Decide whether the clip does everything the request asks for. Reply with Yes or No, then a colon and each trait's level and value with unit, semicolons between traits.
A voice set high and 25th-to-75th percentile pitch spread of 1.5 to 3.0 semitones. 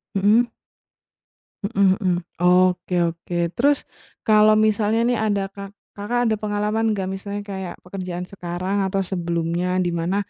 Yes: high, 195 Hz; average, 2.7 semitones